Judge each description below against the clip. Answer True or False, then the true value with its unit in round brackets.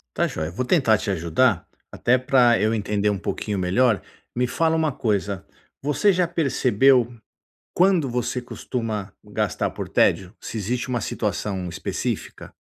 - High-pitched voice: False (120 Hz)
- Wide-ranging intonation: False (4.3 semitones)